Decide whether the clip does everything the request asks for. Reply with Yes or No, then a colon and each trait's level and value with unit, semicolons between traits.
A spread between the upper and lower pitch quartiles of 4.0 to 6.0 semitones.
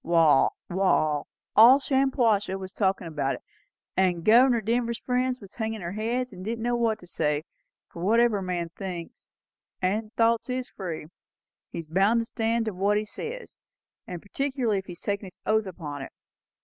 Yes: average, 4.6 semitones